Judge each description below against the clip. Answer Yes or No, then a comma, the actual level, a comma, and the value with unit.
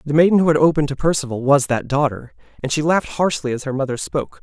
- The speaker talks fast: Yes, fast, 245 wpm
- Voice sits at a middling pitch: Yes, medium, 145 Hz